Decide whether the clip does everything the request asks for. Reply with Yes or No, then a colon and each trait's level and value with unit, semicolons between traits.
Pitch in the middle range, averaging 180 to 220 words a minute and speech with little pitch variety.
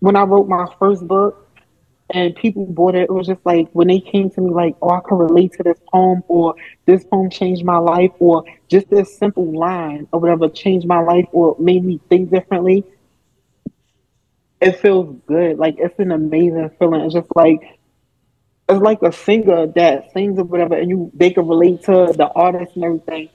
Yes: medium, 175 Hz; average, 200 wpm; narrow, 1.9 semitones